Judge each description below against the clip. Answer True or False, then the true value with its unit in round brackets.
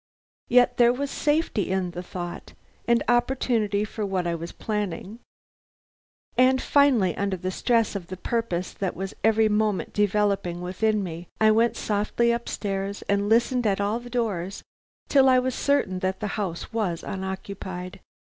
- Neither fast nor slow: True (160 wpm)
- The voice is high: True (205 Hz)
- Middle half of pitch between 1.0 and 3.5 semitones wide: False (4.0 semitones)